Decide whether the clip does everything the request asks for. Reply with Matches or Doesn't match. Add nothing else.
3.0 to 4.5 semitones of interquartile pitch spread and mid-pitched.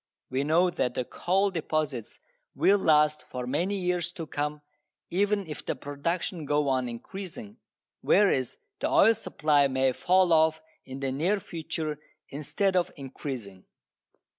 Doesn't match